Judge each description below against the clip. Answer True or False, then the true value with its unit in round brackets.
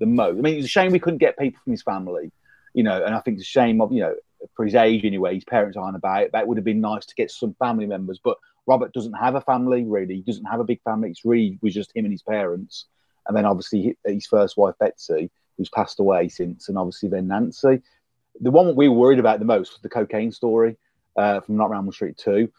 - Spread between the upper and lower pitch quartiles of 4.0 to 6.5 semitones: True (5.1 semitones)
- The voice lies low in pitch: True (115 Hz)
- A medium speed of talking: False (265 wpm)